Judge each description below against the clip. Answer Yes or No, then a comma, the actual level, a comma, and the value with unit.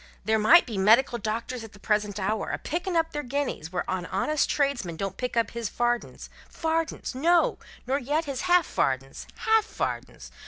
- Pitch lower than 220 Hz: No, high, 240 Hz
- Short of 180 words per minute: No, average, 185 wpm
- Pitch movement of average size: No, wide, 6.6 semitones